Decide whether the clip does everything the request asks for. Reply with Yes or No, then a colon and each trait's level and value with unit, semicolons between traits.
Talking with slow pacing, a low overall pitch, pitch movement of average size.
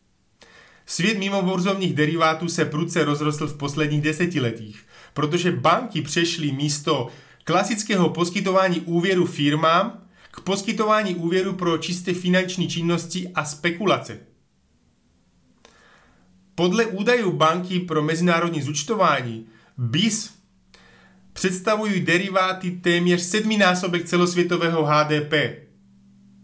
No: slow, 90 wpm; medium, 170 Hz; average, 3.6 semitones